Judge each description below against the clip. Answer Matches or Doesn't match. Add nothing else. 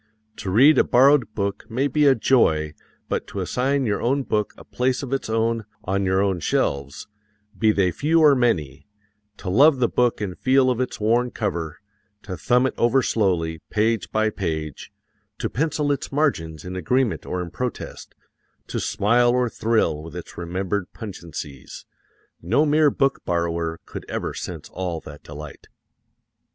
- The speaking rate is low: Doesn't match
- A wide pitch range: Matches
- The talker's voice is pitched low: Matches